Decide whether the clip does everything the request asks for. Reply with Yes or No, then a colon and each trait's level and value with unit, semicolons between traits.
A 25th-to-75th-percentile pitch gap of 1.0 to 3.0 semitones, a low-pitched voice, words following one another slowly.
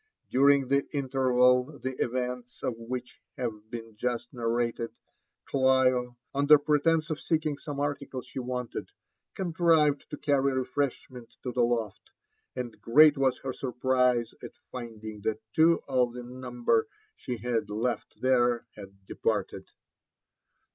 Yes: narrow, 2.6 semitones; low, 125 Hz; slow, 130 wpm